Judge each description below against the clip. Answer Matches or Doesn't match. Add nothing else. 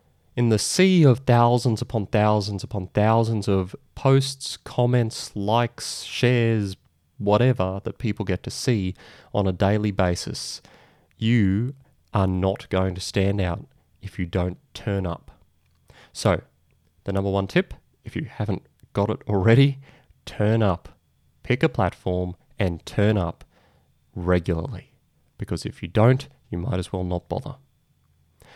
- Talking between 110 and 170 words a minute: Matches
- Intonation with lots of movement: Doesn't match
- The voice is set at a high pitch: Doesn't match